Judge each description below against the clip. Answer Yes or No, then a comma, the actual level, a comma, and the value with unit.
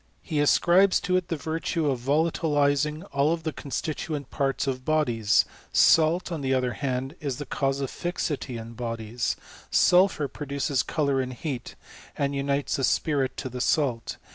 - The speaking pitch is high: No, medium, 140 Hz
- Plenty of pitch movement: No, average, 3.2 semitones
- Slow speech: No, average, 160 wpm